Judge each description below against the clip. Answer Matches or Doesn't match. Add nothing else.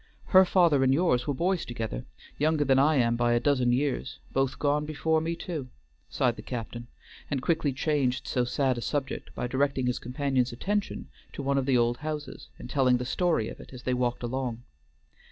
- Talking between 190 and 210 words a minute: Matches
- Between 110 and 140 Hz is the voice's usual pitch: Matches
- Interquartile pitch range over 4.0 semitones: Doesn't match